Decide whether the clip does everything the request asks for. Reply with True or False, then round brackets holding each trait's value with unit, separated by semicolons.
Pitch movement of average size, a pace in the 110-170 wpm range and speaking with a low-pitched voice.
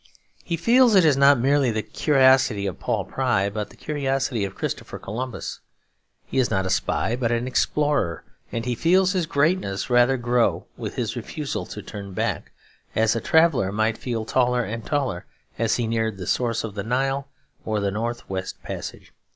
False (4.2 semitones; 185 wpm; 120 Hz)